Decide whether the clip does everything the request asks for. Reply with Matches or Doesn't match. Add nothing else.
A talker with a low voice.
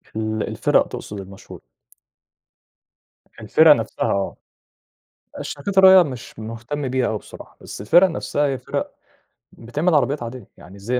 Matches